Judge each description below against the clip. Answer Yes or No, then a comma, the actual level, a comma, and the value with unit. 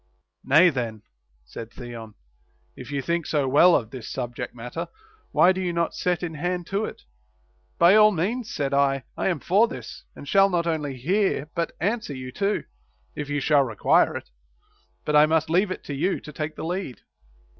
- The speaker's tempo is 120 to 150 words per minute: No, average, 195 wpm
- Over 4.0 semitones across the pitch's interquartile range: Yes, average, 5.1 semitones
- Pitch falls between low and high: Yes, medium, 155 Hz